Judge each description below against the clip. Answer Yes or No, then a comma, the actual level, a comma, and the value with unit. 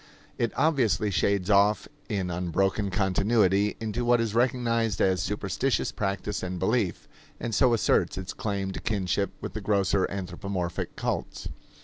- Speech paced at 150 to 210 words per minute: No, average, 140 wpm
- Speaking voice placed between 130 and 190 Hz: No, low, 100 Hz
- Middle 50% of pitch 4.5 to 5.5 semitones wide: No, average, 3.1 semitones